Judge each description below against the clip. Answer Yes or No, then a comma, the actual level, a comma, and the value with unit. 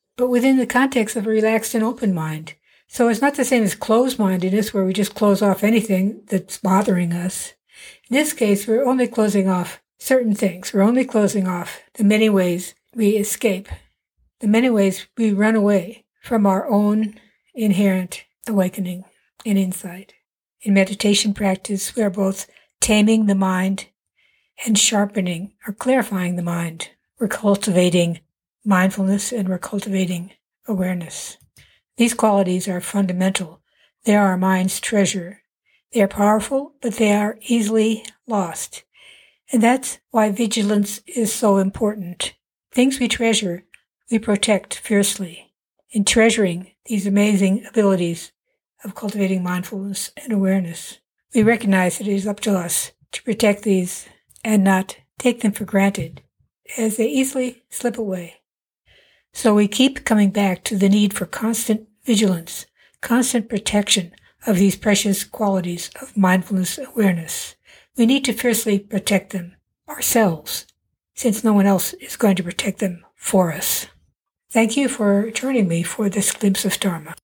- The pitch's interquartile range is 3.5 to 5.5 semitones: No, average, 2.8 semitones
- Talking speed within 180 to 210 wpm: No, average, 150 wpm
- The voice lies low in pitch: No, high, 205 Hz